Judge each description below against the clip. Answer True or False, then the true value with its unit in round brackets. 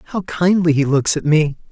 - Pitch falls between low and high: True (160 Hz)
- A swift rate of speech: True (210 wpm)